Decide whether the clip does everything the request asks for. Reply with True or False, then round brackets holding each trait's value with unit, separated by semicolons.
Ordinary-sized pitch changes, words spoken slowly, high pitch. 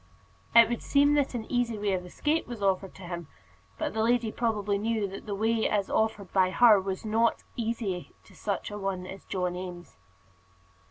False (3.4 semitones; 195 wpm; 210 Hz)